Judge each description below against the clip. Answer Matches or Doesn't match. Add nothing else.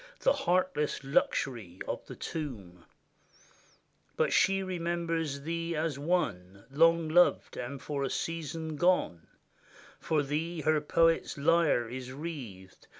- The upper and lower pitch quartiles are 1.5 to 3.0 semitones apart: Doesn't match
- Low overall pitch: Doesn't match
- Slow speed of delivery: Matches